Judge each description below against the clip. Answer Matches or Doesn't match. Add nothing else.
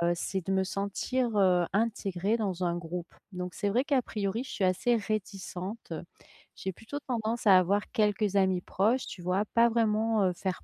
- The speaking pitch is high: Matches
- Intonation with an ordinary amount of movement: Matches